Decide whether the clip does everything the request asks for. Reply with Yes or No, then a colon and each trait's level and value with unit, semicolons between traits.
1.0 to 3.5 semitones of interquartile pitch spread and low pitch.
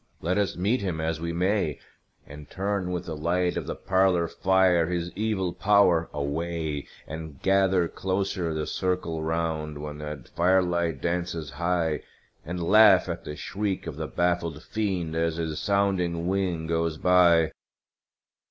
Yes: narrow, 2.6 semitones; very low, 85 Hz